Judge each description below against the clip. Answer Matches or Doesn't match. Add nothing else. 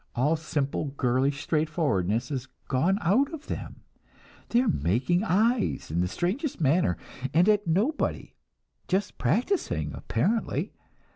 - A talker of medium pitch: Matches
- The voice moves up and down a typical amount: Doesn't match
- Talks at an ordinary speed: Doesn't match